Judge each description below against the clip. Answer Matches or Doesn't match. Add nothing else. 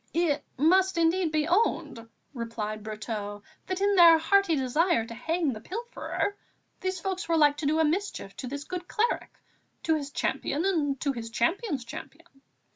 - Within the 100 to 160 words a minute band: Doesn't match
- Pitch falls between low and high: Doesn't match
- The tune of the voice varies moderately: Doesn't match